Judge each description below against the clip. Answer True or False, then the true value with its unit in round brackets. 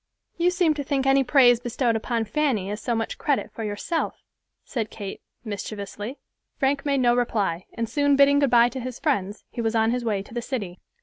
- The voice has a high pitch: True (240 Hz)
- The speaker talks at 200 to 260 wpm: True (205 wpm)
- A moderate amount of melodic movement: True (4.1 semitones)